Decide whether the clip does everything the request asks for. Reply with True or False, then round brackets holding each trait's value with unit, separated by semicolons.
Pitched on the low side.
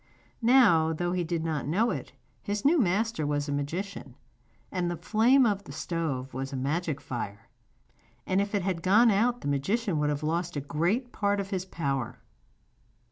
False (175 Hz)